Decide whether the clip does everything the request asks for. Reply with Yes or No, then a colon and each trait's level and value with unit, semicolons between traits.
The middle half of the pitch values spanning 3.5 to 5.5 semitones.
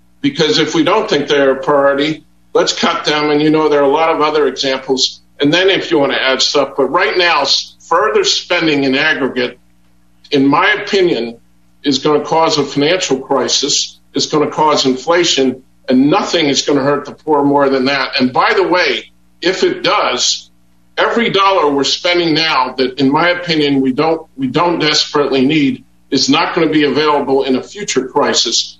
No: average, 3.1 semitones